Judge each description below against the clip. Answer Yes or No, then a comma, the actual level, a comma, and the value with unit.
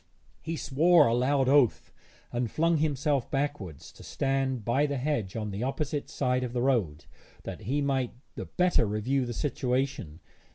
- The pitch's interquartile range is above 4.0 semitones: No, average, 3.5 semitones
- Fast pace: No, average, 165 wpm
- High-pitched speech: No, low, 135 Hz